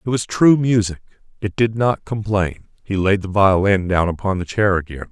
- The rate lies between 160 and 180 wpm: No, average, 200 wpm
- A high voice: No, low, 100 Hz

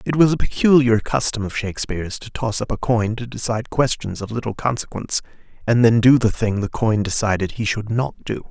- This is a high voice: No, low, 115 Hz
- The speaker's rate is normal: No, fast, 210 wpm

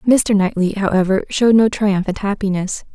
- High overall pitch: Yes, high, 200 Hz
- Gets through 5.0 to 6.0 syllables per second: Yes, 5.3 syllables/s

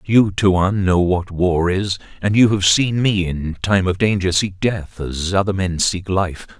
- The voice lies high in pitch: No, very low, 95 Hz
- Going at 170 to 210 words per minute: Yes, average, 200 wpm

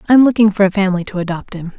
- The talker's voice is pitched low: No, high, 200 Hz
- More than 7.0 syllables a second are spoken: Yes, 8.2 syllables/s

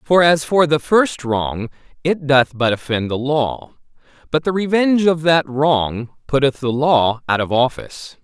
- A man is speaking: Yes, male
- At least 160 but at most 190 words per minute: Yes, average, 175 wpm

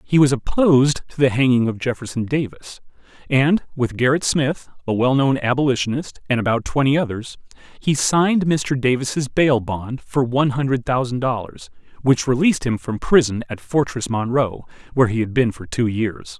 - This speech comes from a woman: No, male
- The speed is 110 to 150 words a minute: No, average, 170 wpm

